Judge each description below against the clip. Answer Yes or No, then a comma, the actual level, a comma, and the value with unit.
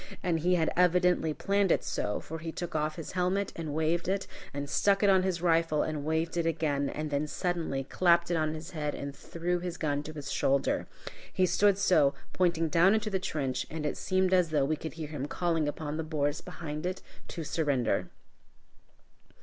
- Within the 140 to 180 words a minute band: No, fast, 205 wpm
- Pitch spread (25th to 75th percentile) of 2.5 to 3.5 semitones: Yes, average, 3.0 semitones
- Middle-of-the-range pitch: Yes, medium, 160 Hz